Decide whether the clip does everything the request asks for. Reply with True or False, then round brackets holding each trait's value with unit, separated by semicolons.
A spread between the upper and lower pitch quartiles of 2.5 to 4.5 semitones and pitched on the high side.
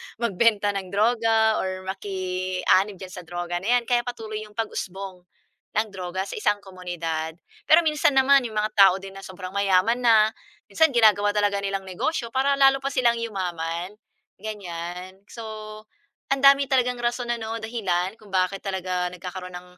True (4.1 semitones; 200 Hz)